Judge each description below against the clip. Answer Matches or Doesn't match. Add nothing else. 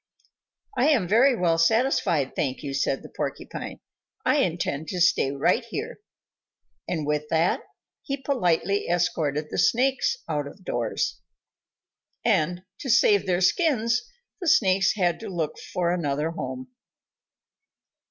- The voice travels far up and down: Matches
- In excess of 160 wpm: Doesn't match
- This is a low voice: Doesn't match